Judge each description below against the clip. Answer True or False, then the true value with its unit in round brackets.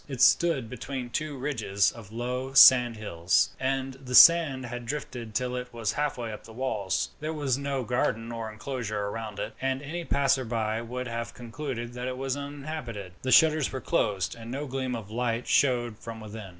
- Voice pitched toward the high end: False (125 Hz)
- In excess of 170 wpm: True (185 wpm)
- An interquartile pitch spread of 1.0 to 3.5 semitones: True (3.0 semitones)